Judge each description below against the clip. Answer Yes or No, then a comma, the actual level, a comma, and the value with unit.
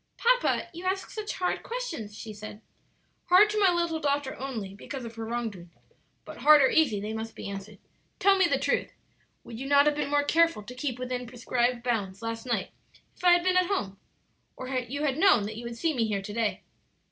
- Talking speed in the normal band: No, fast, 225 wpm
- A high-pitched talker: Yes, very high, 255 Hz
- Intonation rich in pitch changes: Yes, wide, 6.9 semitones